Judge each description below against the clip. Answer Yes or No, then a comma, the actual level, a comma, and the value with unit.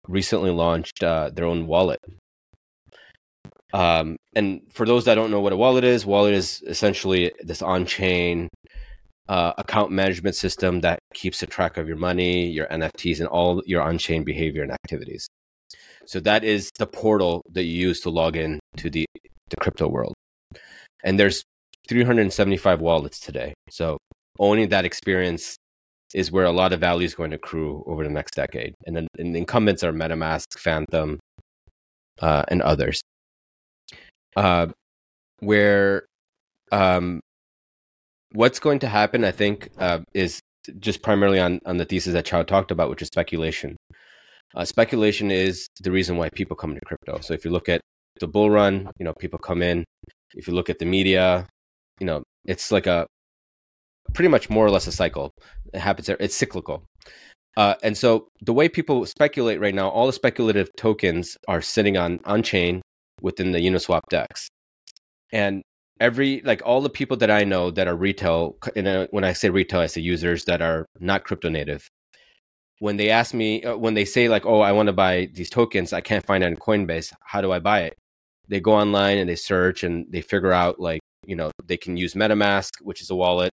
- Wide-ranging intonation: No, average, 3.3 semitones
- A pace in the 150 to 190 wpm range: Yes, average, 185 wpm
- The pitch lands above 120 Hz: No, very low, 90 Hz